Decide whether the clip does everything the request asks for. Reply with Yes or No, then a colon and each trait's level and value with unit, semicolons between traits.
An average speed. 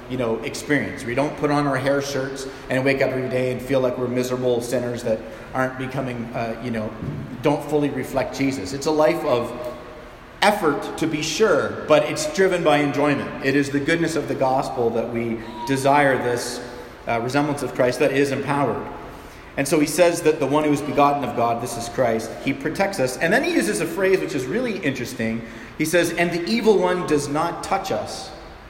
No: fast, 210 wpm